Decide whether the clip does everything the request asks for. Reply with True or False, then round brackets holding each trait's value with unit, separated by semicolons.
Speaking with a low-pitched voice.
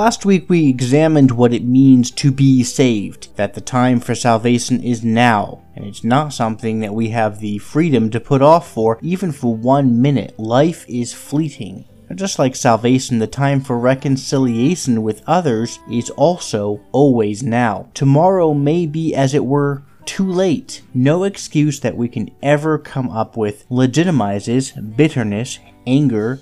True (125 Hz)